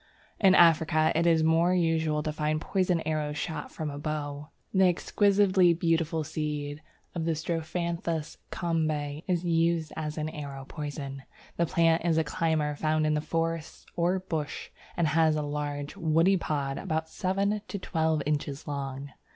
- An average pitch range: No, narrow, 2.0 semitones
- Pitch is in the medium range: Yes, medium, 160 Hz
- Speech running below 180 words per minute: Yes, average, 150 wpm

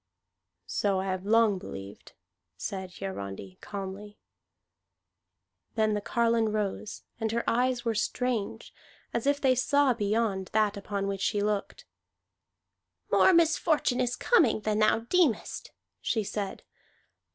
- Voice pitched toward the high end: Yes, high, 215 Hz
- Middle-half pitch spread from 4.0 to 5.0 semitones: No, average, 3.4 semitones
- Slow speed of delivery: Yes, slow, 125 wpm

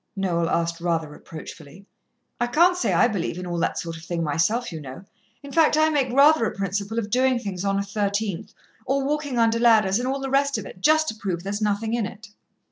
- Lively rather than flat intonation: Yes, wide, 6.2 semitones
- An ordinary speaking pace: No, fast, 225 wpm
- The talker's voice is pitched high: Yes, high, 210 Hz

